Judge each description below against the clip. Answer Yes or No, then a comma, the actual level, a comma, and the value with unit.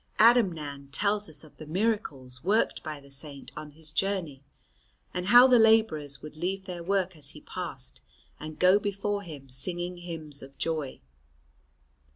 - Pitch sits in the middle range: Yes, medium, 165 Hz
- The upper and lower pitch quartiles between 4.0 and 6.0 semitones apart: Yes, average, 5.2 semitones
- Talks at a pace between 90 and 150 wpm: No, average, 160 wpm